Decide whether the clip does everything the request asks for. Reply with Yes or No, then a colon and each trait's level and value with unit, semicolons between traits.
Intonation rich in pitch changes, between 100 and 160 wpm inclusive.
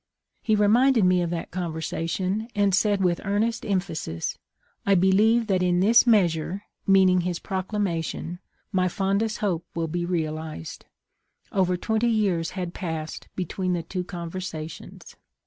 No: average, 3.0 semitones; average, 140 wpm